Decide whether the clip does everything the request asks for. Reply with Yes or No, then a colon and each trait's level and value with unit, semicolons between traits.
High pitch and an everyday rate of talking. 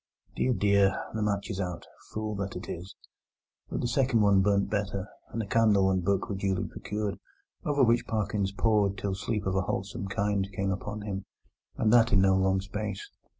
No: low, 100 Hz; average, 195 wpm